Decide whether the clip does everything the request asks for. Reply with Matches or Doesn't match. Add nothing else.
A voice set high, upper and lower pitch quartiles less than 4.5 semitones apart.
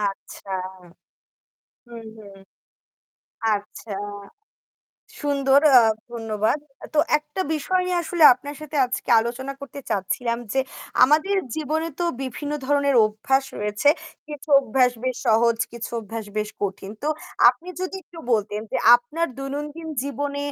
Doesn't match